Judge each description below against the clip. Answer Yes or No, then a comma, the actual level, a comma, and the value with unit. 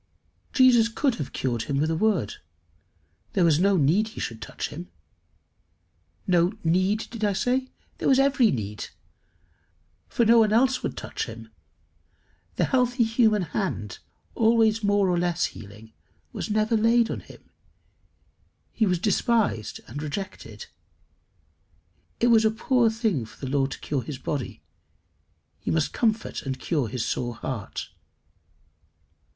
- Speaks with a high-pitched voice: Yes, high, 195 Hz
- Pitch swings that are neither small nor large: No, wide, 8.6 semitones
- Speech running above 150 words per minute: No, average, 145 wpm